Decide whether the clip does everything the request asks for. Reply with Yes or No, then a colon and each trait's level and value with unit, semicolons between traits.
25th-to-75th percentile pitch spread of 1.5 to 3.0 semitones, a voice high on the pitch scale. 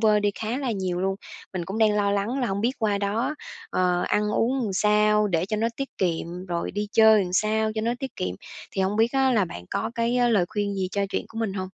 Yes: average, 2.7 semitones; high, 210 Hz